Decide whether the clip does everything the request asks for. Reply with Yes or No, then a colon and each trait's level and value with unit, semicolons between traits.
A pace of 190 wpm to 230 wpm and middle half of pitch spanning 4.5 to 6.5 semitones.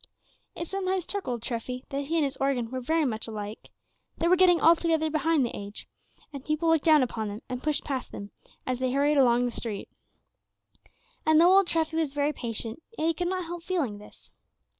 Yes: fast, 205 wpm; average, 5.2 semitones